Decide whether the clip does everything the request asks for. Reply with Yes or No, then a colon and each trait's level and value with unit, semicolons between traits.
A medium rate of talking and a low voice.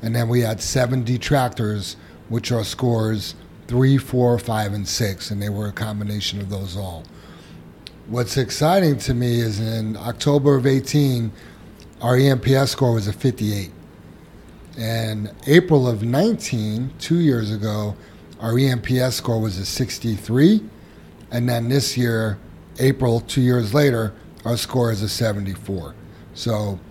Yes: average, 145 wpm; low, 115 Hz